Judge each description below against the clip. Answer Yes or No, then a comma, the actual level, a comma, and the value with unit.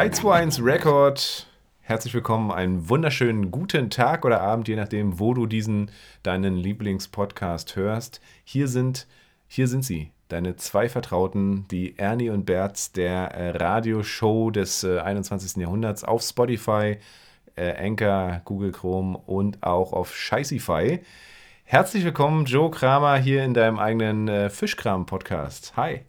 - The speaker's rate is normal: Yes, average, 135 wpm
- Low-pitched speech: Yes, low, 105 Hz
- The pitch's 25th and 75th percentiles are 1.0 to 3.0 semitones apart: No, average, 4.3 semitones